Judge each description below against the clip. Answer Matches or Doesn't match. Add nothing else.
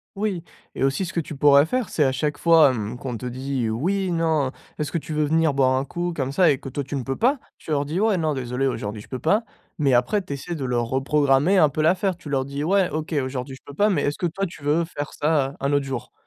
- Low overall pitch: Doesn't match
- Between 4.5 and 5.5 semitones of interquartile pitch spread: Doesn't match